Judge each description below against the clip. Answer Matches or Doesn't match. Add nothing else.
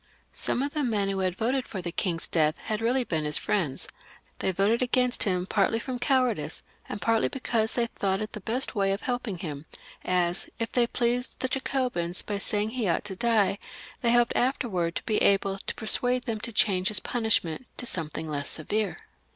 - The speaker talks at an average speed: Matches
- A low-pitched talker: Doesn't match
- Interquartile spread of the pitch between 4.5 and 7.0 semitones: Matches